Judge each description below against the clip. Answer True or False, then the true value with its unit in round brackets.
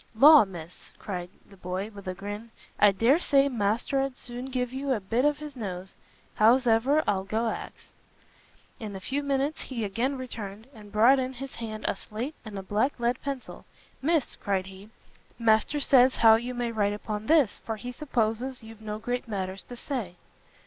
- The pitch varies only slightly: False (4.3 semitones)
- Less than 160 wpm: False (185 wpm)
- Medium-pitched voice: False (230 Hz)